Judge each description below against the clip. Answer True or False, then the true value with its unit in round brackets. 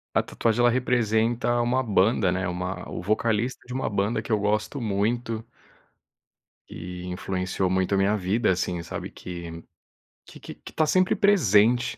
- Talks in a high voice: False (105 Hz)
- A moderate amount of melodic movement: True (4.4 semitones)